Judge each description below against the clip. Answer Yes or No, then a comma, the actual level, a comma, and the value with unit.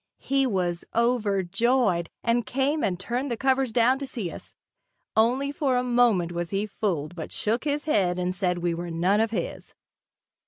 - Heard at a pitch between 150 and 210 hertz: No, high, 220 Hz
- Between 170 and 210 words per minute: Yes, average, 180 wpm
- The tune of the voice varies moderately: No, wide, 5.9 semitones